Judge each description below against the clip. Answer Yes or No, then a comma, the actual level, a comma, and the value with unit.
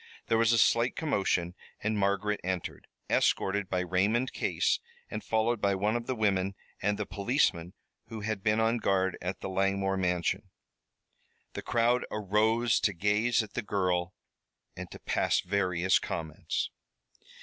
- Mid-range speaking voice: No, low, 100 Hz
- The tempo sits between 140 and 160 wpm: Yes, average, 150 wpm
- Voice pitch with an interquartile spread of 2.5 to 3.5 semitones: Yes, average, 3.0 semitones